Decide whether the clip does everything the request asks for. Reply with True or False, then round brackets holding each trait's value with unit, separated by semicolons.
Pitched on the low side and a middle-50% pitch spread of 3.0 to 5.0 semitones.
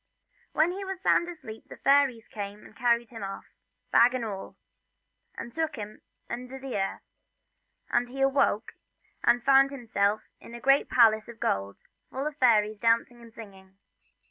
False (235 Hz; 4.0 semitones)